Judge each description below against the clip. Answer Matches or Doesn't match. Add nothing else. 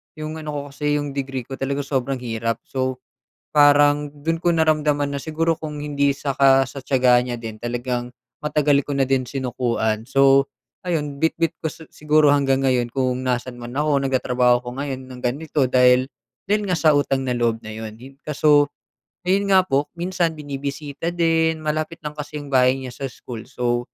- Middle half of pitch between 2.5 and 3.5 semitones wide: Matches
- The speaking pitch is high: Doesn't match